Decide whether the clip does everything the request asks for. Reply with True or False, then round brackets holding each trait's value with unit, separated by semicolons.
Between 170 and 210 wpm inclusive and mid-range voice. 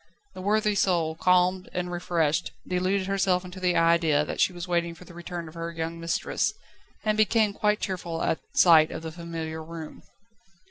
True (180 wpm; 175 Hz)